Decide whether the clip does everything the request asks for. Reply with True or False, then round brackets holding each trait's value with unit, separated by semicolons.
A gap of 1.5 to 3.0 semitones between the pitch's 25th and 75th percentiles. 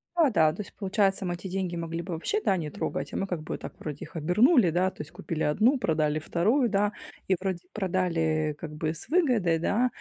False (4.5 semitones)